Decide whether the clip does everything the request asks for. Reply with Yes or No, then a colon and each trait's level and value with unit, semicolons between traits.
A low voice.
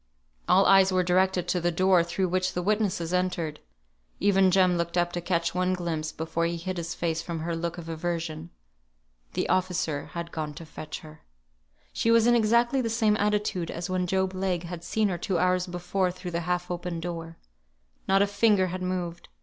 No: medium, 180 Hz